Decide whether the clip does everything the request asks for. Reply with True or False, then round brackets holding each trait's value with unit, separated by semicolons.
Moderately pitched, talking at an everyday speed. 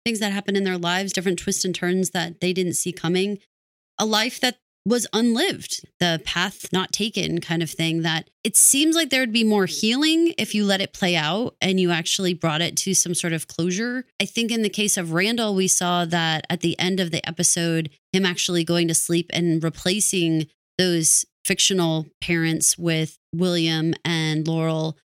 True (180 Hz; 195 wpm)